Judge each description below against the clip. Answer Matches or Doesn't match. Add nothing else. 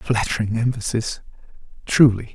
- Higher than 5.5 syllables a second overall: Doesn't match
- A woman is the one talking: Doesn't match